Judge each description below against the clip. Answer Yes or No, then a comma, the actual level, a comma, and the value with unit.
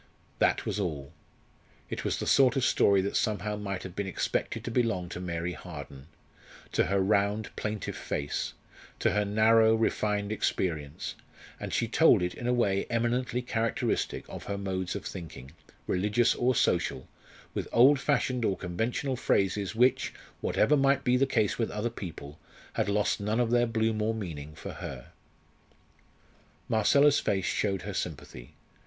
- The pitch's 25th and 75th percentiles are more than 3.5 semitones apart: Yes, average, 4.4 semitones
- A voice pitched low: Yes, low, 105 Hz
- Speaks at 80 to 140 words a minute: No, average, 160 wpm